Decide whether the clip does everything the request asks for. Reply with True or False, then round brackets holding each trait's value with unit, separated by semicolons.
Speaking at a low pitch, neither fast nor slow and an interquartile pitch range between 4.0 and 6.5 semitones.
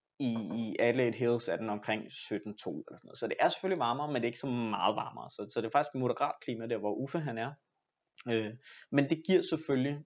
False (125 Hz; 235 wpm; 4.5 semitones)